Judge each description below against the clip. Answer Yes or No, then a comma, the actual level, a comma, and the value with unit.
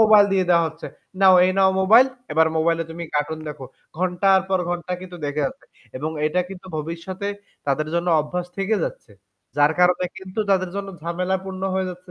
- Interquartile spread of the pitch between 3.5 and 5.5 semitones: No, average, 2.8 semitones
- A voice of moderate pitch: Yes, medium, 180 Hz